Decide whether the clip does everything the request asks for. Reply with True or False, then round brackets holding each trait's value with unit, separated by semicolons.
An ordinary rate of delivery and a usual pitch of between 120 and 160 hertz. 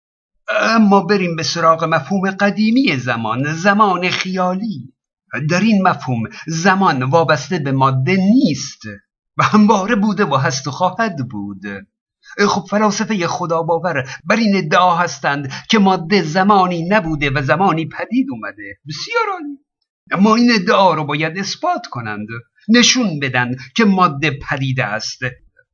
False (130 wpm; 180 Hz)